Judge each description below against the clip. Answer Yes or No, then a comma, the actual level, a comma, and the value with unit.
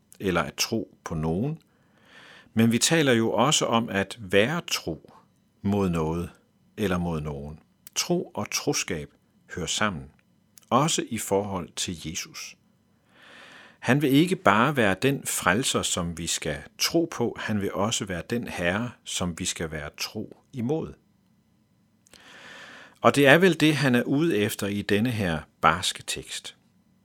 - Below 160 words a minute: Yes, average, 150 wpm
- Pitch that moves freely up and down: Yes, wide, 5.8 semitones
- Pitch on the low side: Yes, low, 100 Hz